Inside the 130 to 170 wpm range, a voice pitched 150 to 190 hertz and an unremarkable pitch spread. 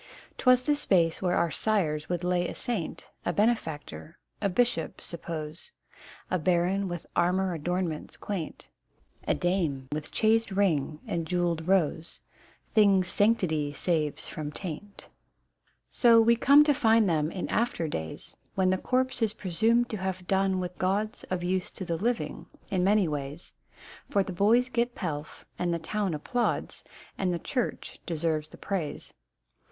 Yes: average, 155 wpm; medium, 185 Hz; average, 4.4 semitones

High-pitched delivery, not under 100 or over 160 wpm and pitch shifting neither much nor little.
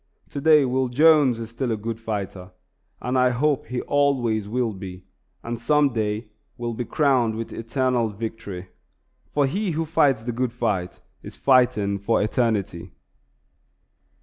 No: low, 120 Hz; average, 150 wpm; average, 3.5 semitones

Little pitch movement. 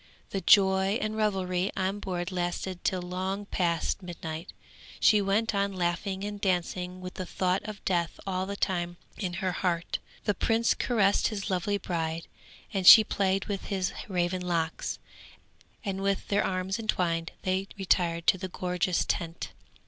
Yes: narrow, 2.0 semitones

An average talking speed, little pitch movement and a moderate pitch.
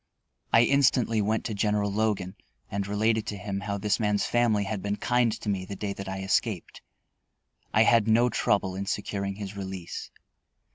No: average, 180 wpm; narrow, 2.0 semitones; low, 105 Hz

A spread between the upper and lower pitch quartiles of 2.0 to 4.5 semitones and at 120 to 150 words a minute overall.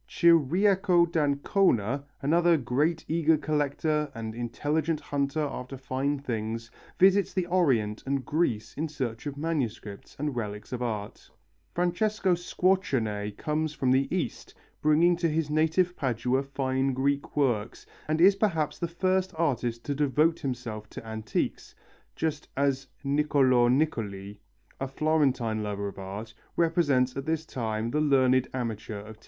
No: average, 5.2 semitones; average, 140 wpm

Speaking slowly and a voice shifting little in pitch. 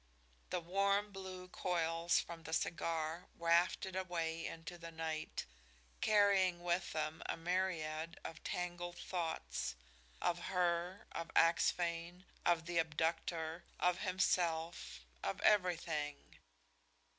Yes: slow, 110 wpm; narrow, 1.8 semitones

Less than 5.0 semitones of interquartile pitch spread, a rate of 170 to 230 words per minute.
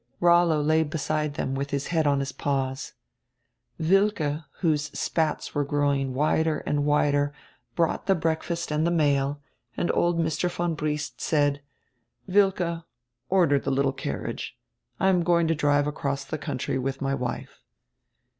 No: average, 2.8 semitones; average, 150 wpm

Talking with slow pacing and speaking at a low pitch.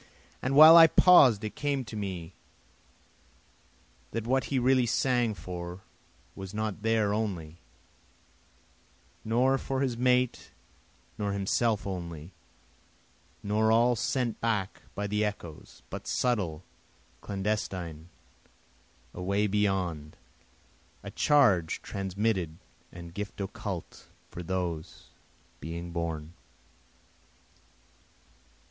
Yes: slow, 100 wpm; low, 105 Hz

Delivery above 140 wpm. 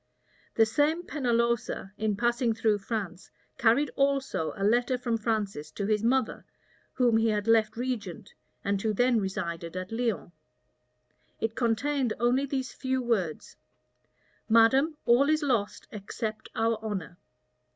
No: slow, 135 wpm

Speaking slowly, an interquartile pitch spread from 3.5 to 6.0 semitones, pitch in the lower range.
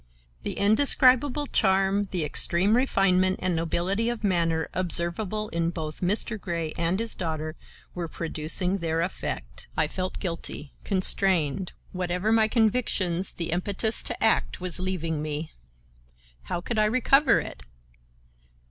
No: slow, 130 wpm; average, 4.1 semitones; medium, 185 Hz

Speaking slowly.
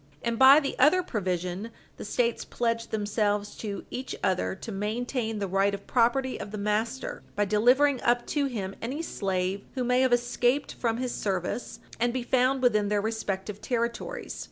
No: average, 175 wpm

